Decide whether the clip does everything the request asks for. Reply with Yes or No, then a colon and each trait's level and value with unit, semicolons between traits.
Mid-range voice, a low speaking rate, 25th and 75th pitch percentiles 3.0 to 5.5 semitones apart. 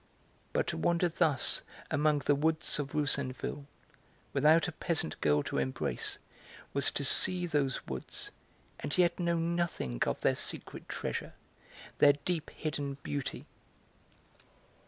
Yes: medium, 145 Hz; slow, 130 wpm; average, 3.3 semitones